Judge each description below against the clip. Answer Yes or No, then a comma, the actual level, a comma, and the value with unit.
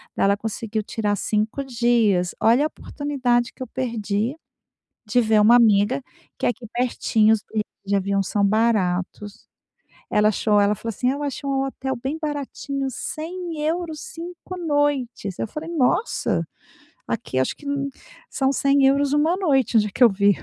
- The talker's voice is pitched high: Yes, high, 240 Hz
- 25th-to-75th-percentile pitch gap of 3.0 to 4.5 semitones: No, average, 5.2 semitones